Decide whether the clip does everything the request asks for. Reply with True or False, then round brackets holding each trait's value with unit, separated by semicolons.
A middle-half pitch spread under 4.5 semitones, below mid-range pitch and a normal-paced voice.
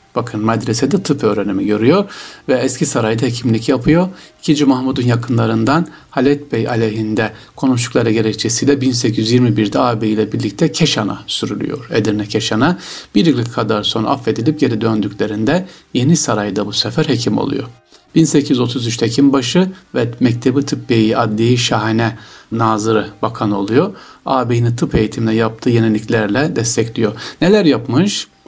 True (3.7 semitones; 120 Hz; 120 wpm)